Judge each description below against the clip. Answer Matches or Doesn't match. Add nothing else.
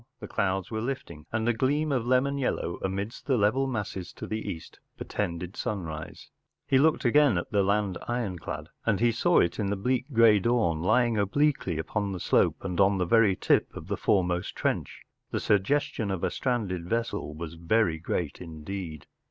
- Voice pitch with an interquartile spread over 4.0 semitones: Matches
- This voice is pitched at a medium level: Doesn't match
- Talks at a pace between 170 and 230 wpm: Matches